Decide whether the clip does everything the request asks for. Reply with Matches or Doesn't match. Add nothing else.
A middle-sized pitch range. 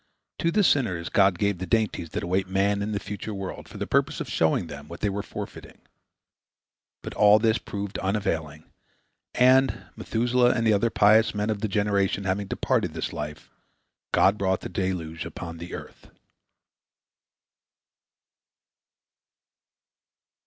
Matches